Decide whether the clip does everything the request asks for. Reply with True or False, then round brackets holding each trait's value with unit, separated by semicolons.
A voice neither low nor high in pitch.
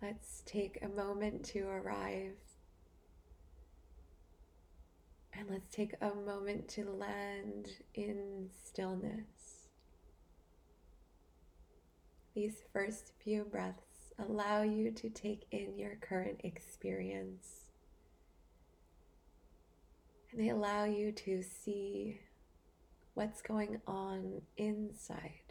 False (100 Hz)